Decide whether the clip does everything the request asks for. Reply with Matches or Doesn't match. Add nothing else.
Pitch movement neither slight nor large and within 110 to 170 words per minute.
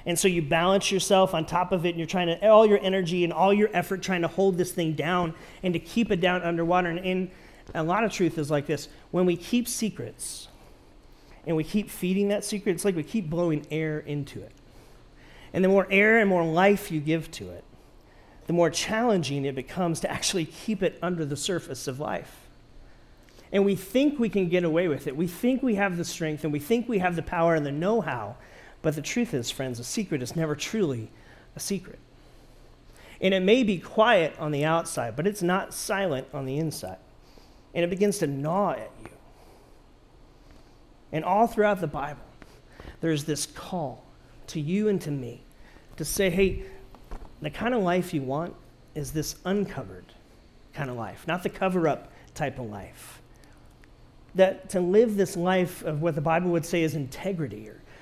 Doesn't match